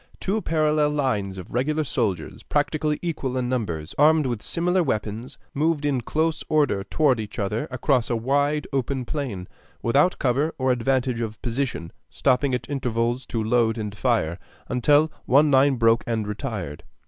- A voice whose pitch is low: Yes, low, 130 Hz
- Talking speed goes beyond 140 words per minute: Yes, average, 160 wpm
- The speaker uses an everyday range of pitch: Yes, average, 4.5 semitones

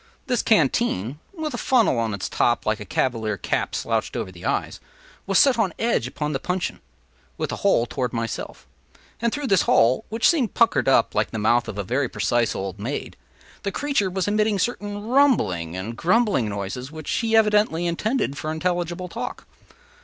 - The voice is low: No, medium, 160 Hz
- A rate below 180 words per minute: No, average, 185 wpm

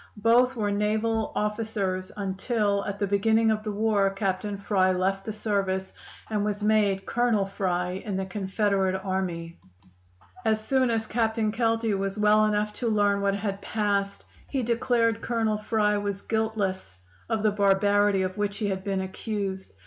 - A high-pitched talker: Yes, high, 205 Hz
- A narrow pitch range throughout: Yes, narrow, 2.0 semitones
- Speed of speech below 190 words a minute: Yes, average, 160 wpm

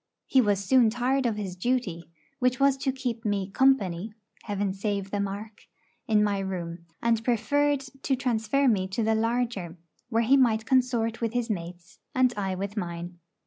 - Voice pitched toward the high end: Yes, high, 220 Hz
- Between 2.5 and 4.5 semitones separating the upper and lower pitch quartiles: Yes, average, 4.2 semitones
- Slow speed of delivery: No, average, 175 wpm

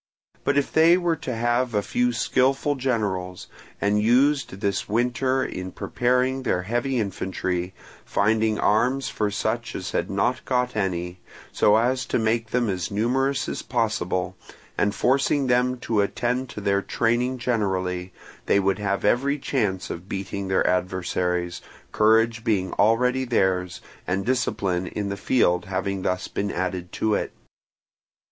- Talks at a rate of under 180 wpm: Yes, average, 150 wpm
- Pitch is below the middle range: Yes, low, 110 Hz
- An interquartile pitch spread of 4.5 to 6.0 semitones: Yes, average, 4.8 semitones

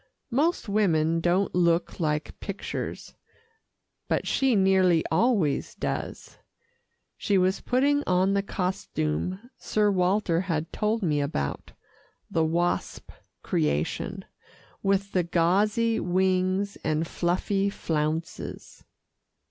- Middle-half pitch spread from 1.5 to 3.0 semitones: No, average, 3.4 semitones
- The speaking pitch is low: No, medium, 185 Hz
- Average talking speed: No, slow, 100 wpm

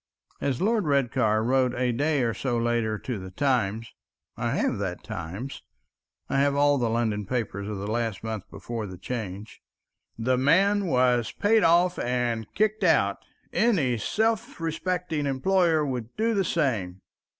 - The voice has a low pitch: Yes, low, 125 Hz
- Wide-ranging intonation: Yes, wide, 6.5 semitones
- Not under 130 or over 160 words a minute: Yes, average, 150 wpm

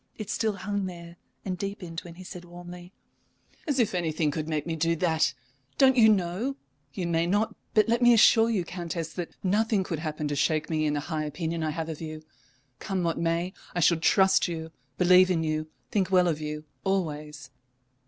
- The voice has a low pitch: No, medium, 175 Hz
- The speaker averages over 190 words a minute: Yes, average, 200 wpm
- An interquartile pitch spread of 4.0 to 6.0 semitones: No, average, 3.3 semitones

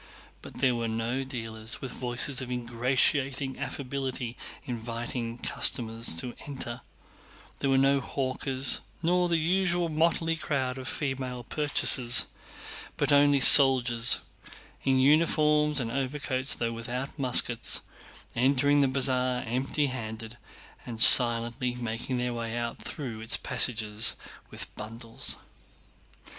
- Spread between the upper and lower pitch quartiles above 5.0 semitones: No, average, 2.8 semitones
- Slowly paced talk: Yes, slow, 115 wpm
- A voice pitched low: Yes, low, 130 Hz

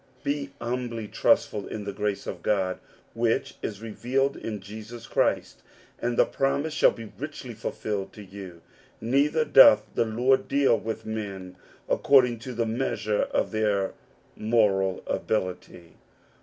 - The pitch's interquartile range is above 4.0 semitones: No, average, 3.7 semitones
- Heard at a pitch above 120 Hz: No, low, 110 Hz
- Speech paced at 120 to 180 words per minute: Yes, average, 140 wpm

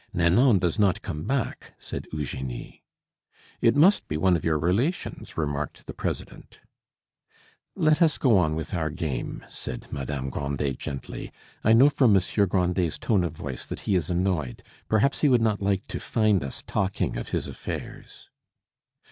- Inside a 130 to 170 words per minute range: Yes, average, 165 wpm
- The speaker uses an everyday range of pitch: No, wide, 6.5 semitones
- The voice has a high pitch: No, very low, 90 Hz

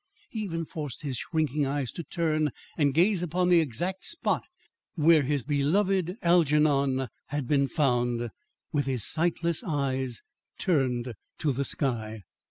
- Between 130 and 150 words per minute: Yes, average, 140 wpm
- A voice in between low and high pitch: Yes, medium, 150 Hz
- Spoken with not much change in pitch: No, average, 4.1 semitones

